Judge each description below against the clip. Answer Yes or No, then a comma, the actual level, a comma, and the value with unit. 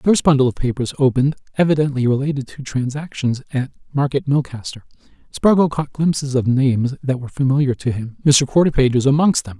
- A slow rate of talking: No, average, 170 wpm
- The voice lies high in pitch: No, low, 135 Hz